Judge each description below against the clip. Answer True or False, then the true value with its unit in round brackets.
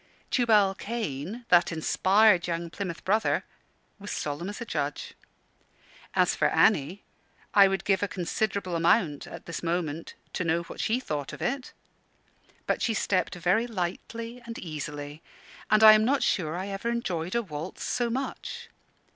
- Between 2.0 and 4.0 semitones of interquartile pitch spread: False (4.8 semitones)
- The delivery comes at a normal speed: True (155 wpm)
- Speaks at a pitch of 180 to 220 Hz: True (190 Hz)